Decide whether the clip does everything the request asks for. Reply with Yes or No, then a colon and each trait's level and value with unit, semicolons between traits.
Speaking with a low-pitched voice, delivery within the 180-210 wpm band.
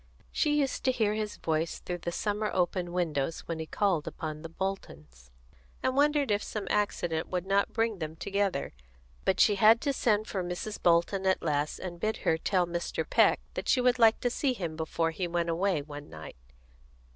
No: medium, 185 Hz; average, 195 wpm